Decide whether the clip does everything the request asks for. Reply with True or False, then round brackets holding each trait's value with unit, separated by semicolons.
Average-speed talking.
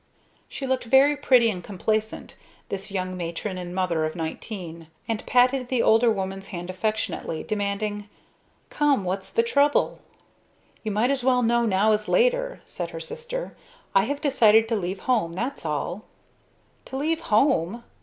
True (155 wpm)